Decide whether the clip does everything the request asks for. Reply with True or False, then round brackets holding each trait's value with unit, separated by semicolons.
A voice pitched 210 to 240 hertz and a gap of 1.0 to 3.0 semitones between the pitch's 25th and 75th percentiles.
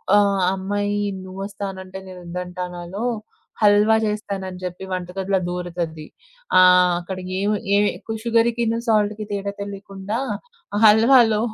False (195 Hz; 2.4 semitones)